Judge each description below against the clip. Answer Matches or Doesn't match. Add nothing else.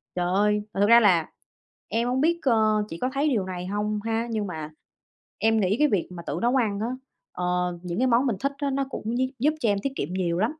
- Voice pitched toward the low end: Doesn't match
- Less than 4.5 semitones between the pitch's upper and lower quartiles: Doesn't match